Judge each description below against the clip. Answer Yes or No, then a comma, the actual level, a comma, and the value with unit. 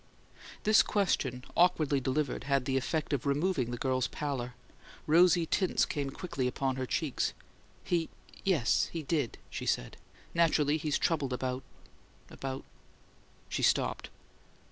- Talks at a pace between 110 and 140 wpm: Yes, slow, 135 wpm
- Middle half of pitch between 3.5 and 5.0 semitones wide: Yes, average, 4.0 semitones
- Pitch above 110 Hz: Yes, medium, 140 Hz